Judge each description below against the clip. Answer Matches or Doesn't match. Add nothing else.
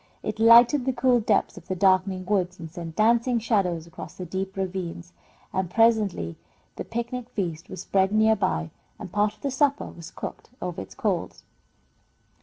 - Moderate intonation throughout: Matches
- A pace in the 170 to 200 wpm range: Matches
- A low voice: Doesn't match